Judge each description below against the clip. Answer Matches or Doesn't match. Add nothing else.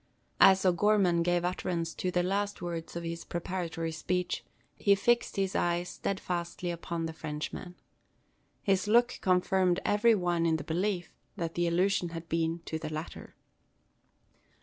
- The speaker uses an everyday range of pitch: Doesn't match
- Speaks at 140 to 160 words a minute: Matches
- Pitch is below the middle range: Doesn't match